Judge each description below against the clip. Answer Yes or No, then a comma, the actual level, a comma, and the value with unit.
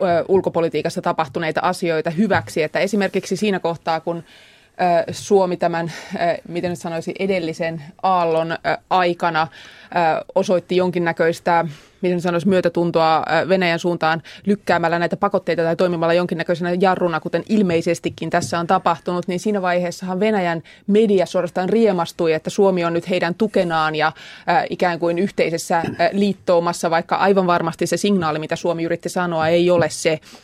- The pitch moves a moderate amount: No, narrow, 1.9 semitones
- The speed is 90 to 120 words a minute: No, average, 130 wpm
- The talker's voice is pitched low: No, medium, 175 Hz